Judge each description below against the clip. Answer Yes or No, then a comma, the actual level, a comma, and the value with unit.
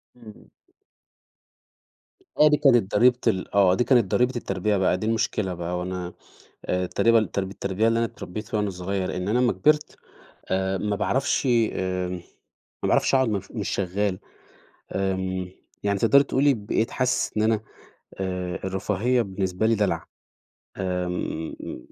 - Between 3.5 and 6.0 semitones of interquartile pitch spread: Yes, average, 3.8 semitones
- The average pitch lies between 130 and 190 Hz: No, low, 100 Hz